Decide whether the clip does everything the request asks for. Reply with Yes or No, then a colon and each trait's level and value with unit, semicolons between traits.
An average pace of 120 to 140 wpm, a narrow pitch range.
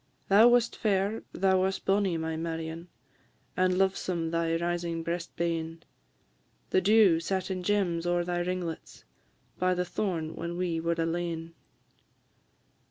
Yes: slow, 135 wpm; narrow, 2.2 semitones